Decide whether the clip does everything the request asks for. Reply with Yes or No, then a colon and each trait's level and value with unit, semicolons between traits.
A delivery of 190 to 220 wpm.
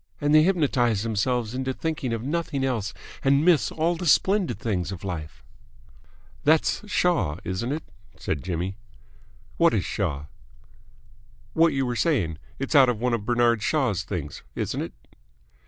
No: average, 155 wpm